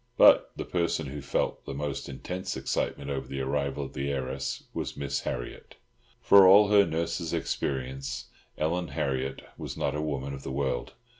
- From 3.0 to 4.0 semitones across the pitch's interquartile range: Yes, average, 3.7 semitones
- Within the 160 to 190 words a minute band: Yes, average, 170 wpm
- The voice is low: Yes, very low, 70 Hz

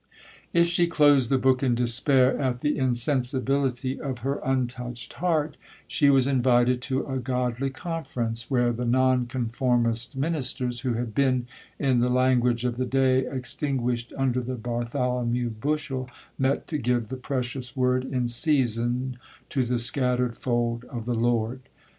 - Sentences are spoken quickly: No, average, 150 wpm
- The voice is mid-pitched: No, low, 125 Hz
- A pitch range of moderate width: No, narrow, 1.7 semitones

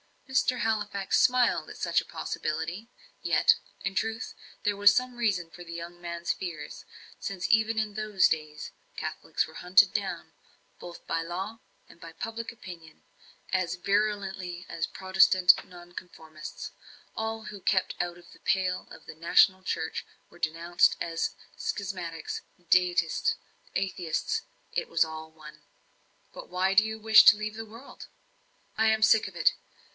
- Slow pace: No, average, 150 wpm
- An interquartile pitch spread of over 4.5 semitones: No, average, 4.0 semitones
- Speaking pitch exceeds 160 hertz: Yes, medium, 185 Hz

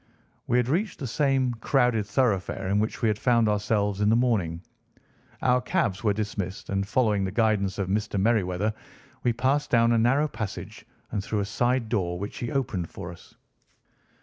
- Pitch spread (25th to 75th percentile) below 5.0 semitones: Yes, average, 3.7 semitones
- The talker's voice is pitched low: Yes, low, 110 Hz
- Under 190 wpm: Yes, average, 180 wpm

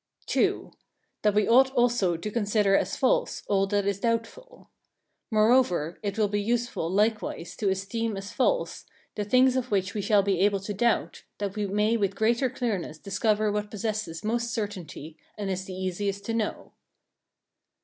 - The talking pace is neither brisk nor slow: Yes, average, 170 wpm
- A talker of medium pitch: No, high, 210 Hz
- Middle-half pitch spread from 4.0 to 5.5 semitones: No, average, 2.7 semitones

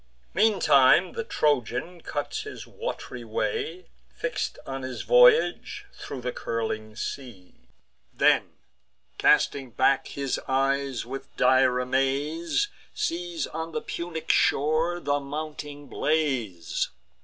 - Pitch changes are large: No, average, 4.2 semitones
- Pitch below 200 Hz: Yes, medium, 140 Hz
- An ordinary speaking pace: No, slow, 110 wpm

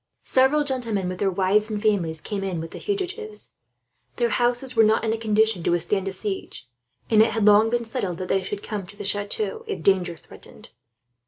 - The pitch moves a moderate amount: Yes, average, 3.8 semitones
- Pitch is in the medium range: No, high, 210 Hz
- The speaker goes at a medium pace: No, fast, 210 wpm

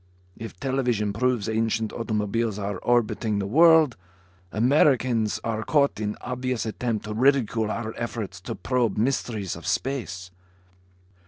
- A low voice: Yes, low, 115 Hz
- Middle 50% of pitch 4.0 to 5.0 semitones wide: No, average, 3.0 semitones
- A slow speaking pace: Yes, slow, 130 wpm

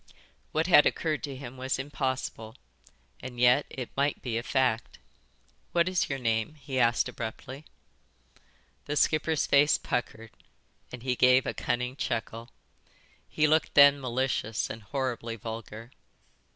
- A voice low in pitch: Yes, low, 130 Hz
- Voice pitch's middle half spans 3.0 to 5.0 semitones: Yes, average, 3.4 semitones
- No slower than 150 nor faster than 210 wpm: No, average, 140 wpm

